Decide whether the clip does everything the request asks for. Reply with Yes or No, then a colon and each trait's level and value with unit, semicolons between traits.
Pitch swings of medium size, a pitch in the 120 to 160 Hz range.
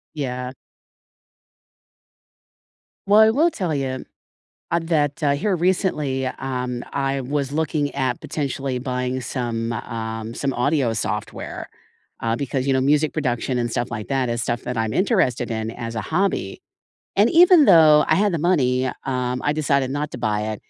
Yes: average, 3.9 semitones; low, 135 Hz